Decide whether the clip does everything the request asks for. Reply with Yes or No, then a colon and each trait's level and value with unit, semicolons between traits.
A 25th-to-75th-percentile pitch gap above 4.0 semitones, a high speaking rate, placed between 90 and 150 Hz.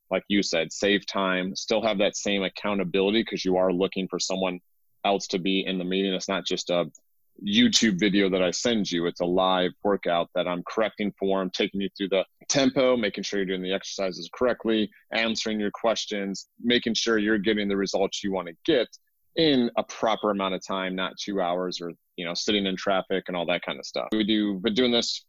No: narrow, 2.6 semitones; fast, 220 wpm; very low, 95 Hz